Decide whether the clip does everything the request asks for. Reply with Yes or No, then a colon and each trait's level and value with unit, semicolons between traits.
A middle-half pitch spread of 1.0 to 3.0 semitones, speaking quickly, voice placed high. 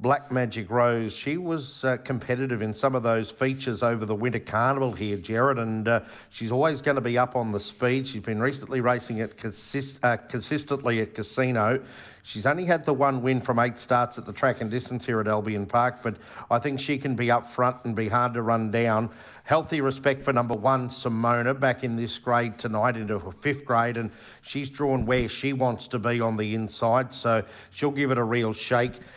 No: average, 2.7 semitones; fast, 215 wpm; low, 120 Hz